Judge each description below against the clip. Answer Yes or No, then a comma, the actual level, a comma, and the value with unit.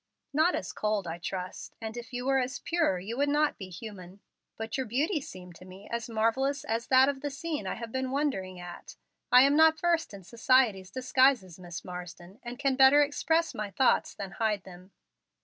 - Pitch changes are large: Yes, wide, 6.4 semitones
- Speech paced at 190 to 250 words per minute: Yes, average, 200 wpm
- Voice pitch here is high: Yes, high, 235 Hz